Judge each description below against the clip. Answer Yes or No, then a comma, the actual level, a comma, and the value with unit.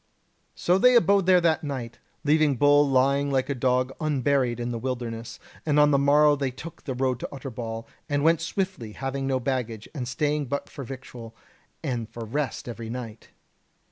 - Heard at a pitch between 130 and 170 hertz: Yes, low, 135 Hz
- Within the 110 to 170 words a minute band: No, average, 180 wpm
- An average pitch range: Yes, average, 3.4 semitones